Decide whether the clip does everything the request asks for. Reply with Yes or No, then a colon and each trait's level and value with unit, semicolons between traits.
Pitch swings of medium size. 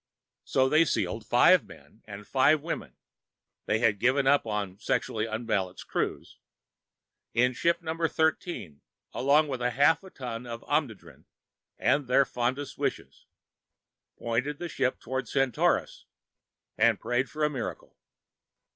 Yes: average, 4.4 semitones